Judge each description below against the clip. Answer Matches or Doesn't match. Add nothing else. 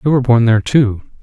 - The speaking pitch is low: Matches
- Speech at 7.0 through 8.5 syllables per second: Matches